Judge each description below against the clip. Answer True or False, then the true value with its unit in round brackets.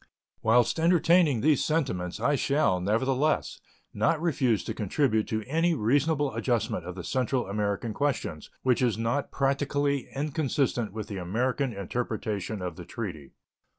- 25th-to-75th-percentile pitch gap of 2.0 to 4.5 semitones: False (5.3 semitones)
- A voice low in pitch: True (125 Hz)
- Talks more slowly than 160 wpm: True (140 wpm)